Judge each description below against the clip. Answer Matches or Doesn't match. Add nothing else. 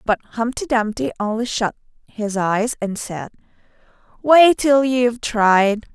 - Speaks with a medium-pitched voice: Doesn't match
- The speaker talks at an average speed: Doesn't match